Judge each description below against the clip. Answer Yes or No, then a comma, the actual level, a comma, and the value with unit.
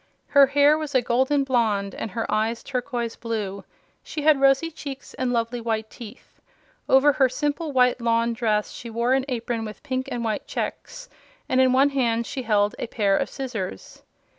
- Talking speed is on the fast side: No, average, 185 wpm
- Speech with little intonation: No, average, 3.1 semitones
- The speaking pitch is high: Yes, high, 245 Hz